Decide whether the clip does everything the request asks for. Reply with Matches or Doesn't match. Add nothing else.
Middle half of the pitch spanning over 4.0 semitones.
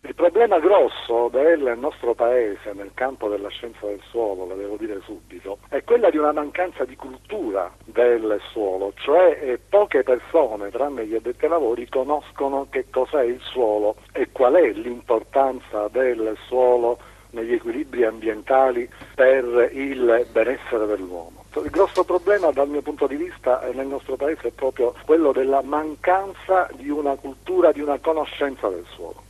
Matches